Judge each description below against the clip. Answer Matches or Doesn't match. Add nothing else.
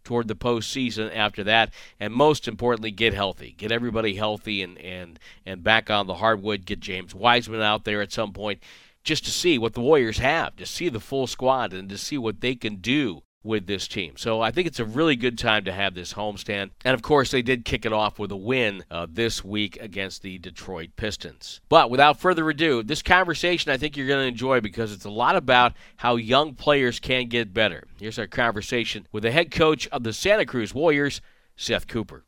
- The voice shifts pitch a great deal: Doesn't match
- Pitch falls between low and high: Doesn't match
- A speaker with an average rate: Doesn't match